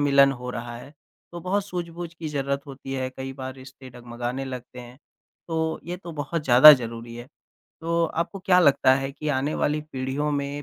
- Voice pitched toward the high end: No, medium, 140 Hz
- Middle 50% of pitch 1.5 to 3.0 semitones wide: No, average, 3.7 semitones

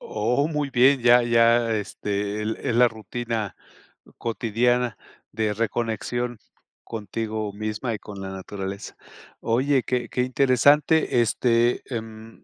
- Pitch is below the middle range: Yes, low, 115 Hz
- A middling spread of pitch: No, narrow, 2.3 semitones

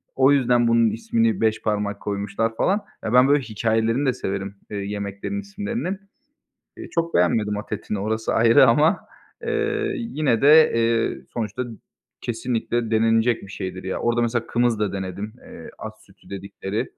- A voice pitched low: Yes, low, 115 Hz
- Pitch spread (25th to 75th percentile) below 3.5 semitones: No, average, 4.4 semitones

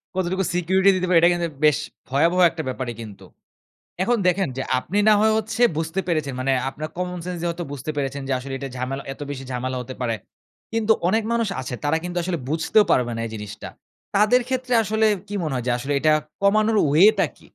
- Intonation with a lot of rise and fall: Yes, wide, 6.3 semitones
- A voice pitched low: No, medium, 165 Hz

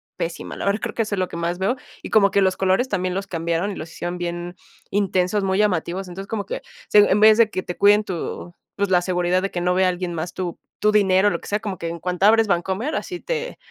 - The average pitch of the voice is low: No, high, 190 Hz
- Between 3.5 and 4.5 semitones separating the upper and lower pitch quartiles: No, narrow, 2.6 semitones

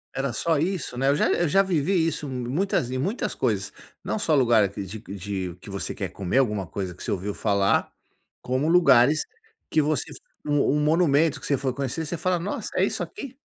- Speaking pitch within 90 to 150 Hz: Yes, medium, 140 Hz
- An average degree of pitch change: No, wide, 7.1 semitones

